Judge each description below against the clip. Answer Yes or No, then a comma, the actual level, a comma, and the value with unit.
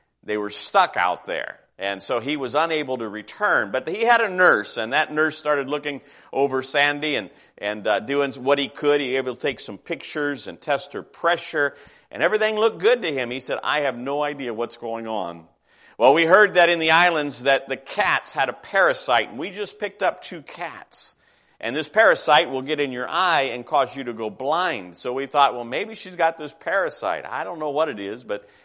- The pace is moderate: No, fast, 225 wpm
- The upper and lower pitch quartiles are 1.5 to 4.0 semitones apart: No, average, 4.5 semitones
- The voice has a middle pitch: Yes, medium, 145 Hz